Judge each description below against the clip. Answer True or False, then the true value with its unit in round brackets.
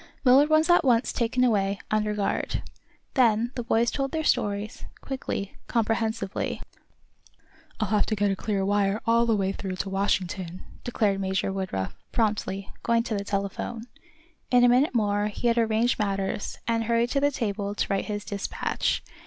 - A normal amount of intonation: True (3.0 semitones)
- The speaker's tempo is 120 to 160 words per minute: False (170 wpm)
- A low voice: False (215 Hz)